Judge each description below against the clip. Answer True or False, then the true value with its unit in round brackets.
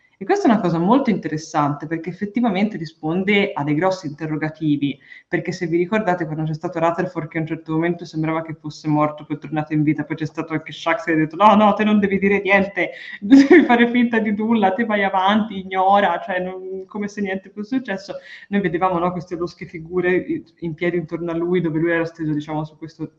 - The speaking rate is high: True (225 wpm)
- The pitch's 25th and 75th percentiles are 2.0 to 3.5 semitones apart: False (4.1 semitones)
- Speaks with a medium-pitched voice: True (175 Hz)